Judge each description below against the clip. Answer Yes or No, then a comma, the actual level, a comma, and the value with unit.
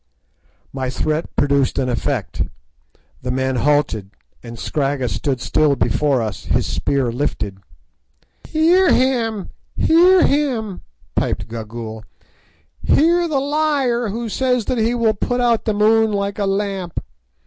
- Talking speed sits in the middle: No, slow, 130 wpm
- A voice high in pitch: Yes, high, 200 Hz